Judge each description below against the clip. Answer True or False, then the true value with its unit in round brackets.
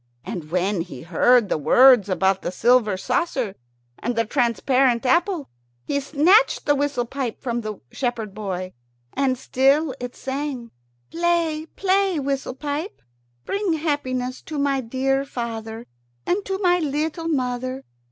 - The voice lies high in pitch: True (260 Hz)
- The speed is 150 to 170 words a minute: False (140 wpm)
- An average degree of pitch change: True (4.3 semitones)